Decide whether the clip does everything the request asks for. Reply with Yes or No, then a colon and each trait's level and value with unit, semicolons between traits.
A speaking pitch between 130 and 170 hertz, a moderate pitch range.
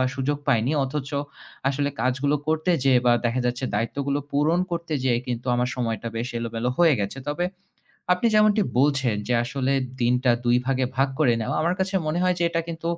Yes: low, 135 Hz; average, 4.3 semitones